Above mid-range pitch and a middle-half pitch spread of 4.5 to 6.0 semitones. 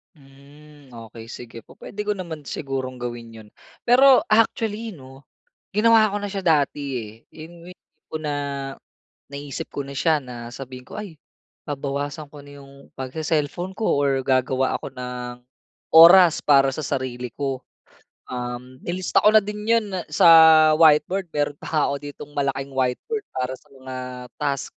No: medium, 145 Hz; average, 4.8 semitones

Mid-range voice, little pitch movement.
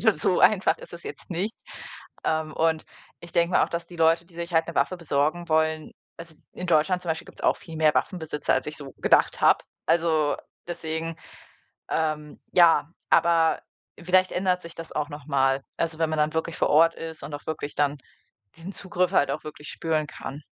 Yes: medium, 160 Hz; narrow, 1.8 semitones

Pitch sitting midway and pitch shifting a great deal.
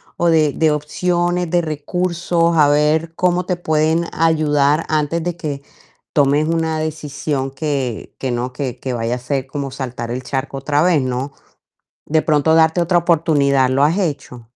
No: medium, 150 Hz; average, 3.2 semitones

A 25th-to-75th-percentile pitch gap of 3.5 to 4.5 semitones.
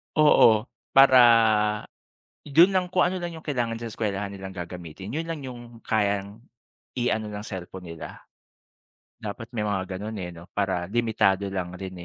Yes: average, 4.1 semitones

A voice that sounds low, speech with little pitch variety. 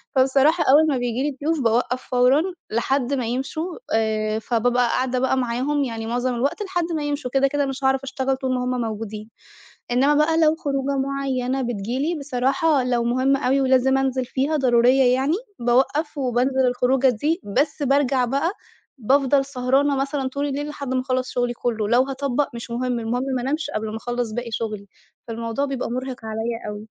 No: very high, 260 Hz; narrow, 2.3 semitones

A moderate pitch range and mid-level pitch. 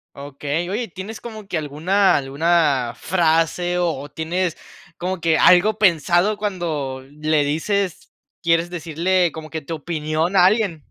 Yes: average, 3.3 semitones; medium, 170 Hz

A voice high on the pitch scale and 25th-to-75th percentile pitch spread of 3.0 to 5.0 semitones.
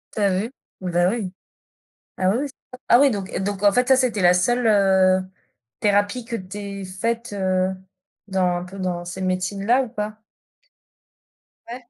Yes: high, 200 Hz; average, 3.5 semitones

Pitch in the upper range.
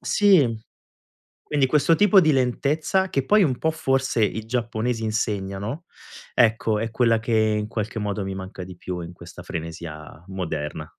No: low, 110 Hz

